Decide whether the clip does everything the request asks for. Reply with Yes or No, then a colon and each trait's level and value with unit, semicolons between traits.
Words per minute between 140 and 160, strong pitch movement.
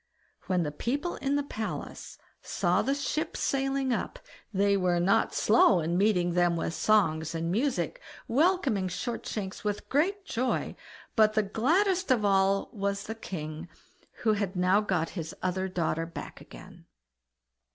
Yes: average, 150 wpm; wide, 6.5 semitones